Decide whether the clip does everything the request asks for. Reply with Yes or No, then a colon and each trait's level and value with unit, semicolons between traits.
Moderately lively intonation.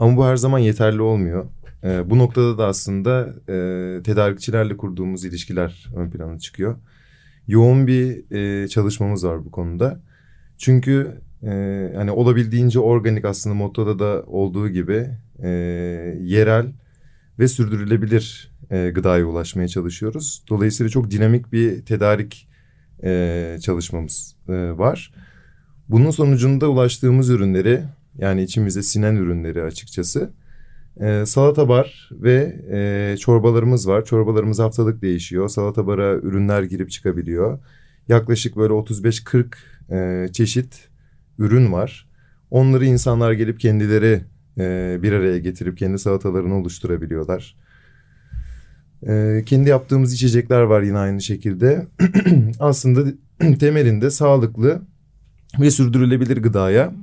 Yes: average, 4.8 semitones